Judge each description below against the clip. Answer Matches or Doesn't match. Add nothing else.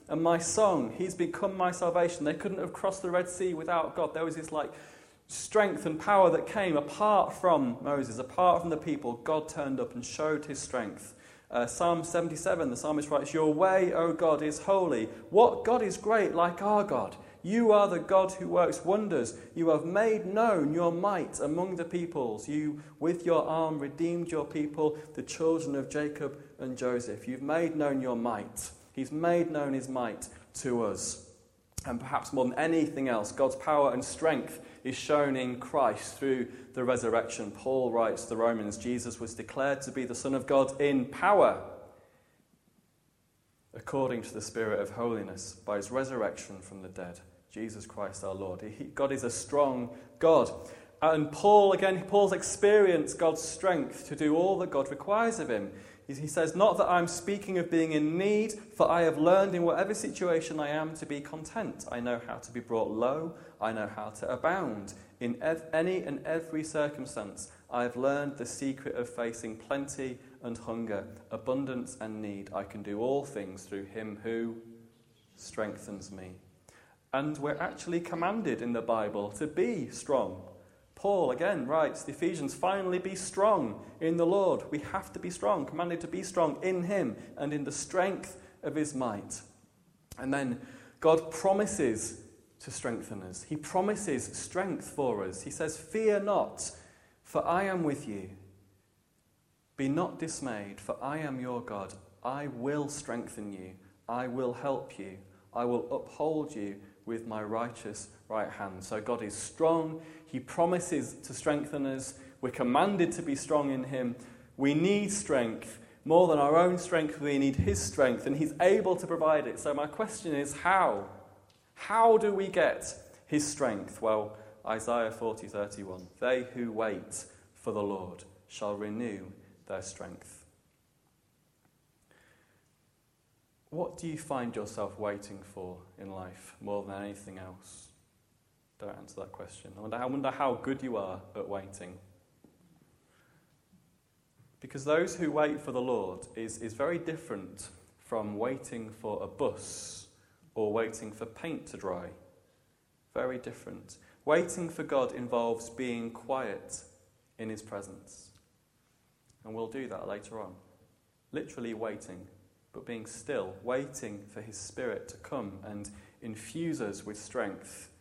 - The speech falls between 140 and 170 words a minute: Matches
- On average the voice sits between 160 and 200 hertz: Doesn't match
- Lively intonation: Matches